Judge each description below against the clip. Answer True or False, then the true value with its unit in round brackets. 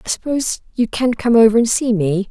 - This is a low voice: False (225 Hz)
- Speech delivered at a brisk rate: True (235 wpm)